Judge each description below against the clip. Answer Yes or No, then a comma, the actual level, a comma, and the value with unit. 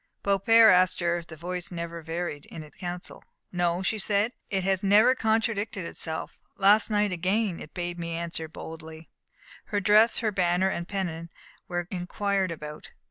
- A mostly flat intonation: No, average, 3.2 semitones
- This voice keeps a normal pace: Yes, average, 165 wpm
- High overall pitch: No, medium, 180 Hz